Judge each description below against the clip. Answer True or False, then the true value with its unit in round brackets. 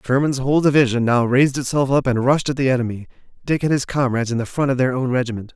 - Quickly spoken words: True (250 wpm)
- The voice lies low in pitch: True (130 Hz)